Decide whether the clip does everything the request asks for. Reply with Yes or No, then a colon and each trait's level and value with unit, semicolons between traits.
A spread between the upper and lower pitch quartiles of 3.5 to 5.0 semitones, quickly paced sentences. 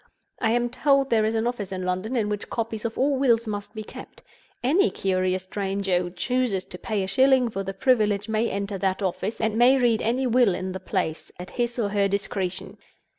Yes: average, 3.9 semitones; fast, 215 wpm